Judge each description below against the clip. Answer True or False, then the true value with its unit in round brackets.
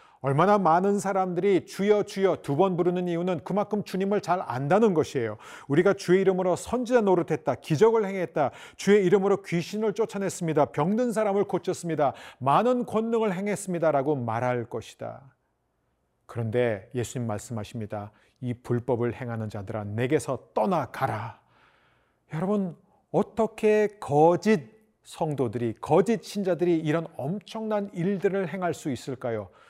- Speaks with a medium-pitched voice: True (175 Hz)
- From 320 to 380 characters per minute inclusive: True (325 characters per minute)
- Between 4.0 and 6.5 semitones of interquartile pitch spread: False (7.1 semitones)